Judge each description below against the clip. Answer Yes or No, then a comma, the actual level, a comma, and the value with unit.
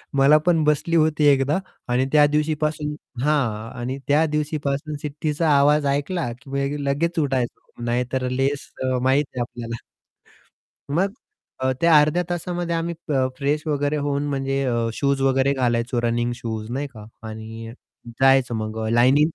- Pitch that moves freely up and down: No, average, 3.3 semitones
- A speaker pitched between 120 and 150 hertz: Yes, medium, 140 Hz